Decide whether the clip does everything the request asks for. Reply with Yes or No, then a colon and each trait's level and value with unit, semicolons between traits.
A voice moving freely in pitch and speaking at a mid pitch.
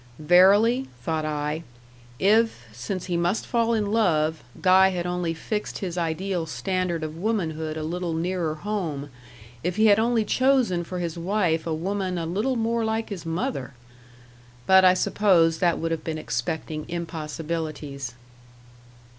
No: average, 4.1 semitones; medium, 175 Hz